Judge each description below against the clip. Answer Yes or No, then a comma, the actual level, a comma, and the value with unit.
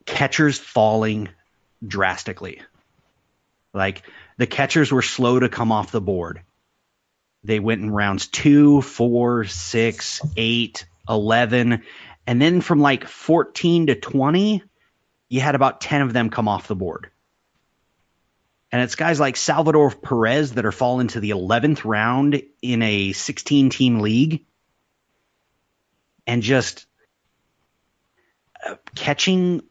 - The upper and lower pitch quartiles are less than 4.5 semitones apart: No, average, 4.8 semitones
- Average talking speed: No, slow, 125 wpm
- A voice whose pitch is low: Yes, low, 120 Hz